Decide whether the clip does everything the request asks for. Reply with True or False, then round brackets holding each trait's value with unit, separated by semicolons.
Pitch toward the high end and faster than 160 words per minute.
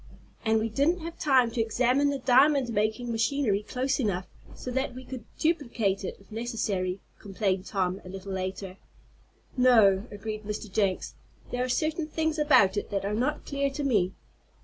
True (225 Hz; 170 wpm)